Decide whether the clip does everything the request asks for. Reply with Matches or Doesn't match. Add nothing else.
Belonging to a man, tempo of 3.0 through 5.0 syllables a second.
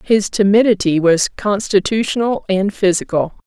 Doesn't match